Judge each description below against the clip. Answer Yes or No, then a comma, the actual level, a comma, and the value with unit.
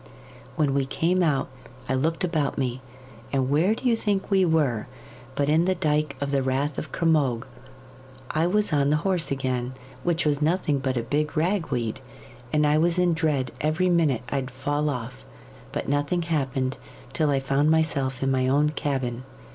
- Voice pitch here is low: No, medium, 145 Hz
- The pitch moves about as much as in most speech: Yes, average, 3.6 semitones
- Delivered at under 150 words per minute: No, average, 180 wpm